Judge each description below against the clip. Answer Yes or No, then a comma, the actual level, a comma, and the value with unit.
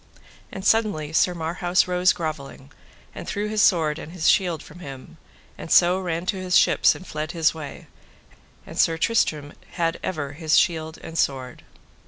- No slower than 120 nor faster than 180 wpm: Yes, average, 175 wpm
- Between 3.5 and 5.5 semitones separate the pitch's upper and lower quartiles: No, average, 3.0 semitones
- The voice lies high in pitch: No, medium, 165 Hz